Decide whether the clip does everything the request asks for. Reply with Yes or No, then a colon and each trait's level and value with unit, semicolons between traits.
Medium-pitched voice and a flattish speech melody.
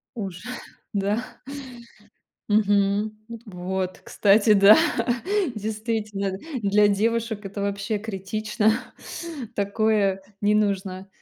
No: high, 205 Hz; narrow, 1.6 semitones